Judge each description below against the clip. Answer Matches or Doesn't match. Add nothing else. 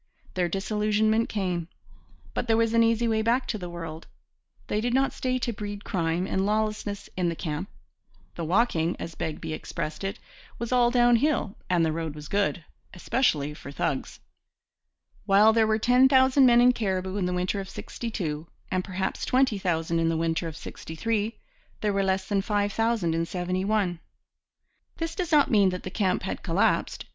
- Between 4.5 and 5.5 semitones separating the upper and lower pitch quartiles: Matches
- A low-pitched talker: Doesn't match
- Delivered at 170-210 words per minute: Matches